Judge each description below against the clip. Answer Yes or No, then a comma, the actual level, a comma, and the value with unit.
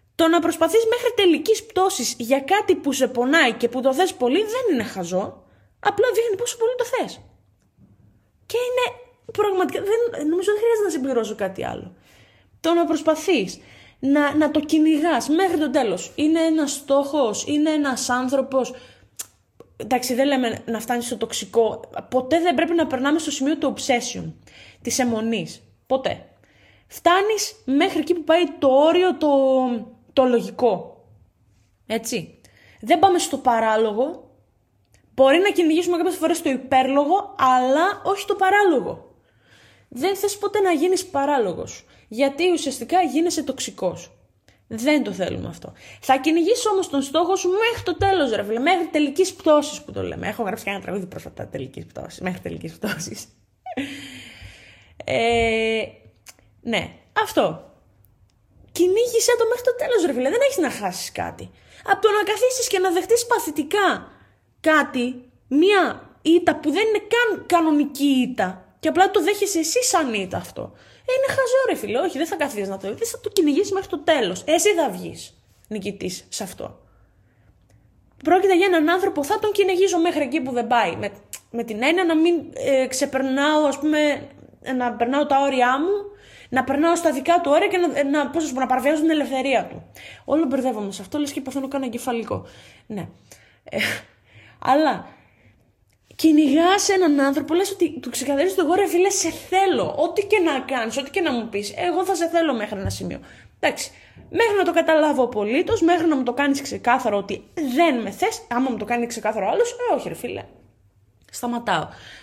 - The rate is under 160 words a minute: No, average, 165 wpm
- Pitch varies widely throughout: Yes, wide, 6.7 semitones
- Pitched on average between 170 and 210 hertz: No, very high, 305 Hz